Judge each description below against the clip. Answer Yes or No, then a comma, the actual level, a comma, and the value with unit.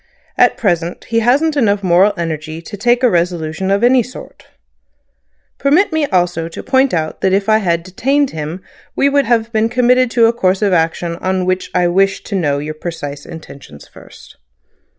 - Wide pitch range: Yes, wide, 6.0 semitones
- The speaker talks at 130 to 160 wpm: No, average, 185 wpm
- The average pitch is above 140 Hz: Yes, high, 190 Hz